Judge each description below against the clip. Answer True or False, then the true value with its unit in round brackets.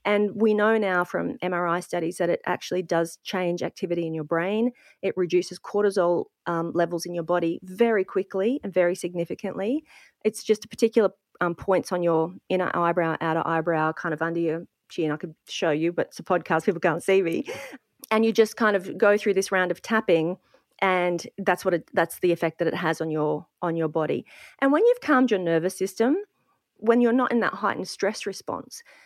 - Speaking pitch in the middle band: True (180 Hz)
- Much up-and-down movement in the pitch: False (4.0 semitones)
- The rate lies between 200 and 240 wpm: True (205 wpm)